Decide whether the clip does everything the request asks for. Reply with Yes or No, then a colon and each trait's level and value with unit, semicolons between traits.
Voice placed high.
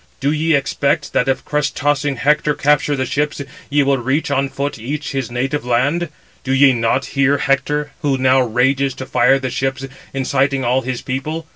No: low, 135 Hz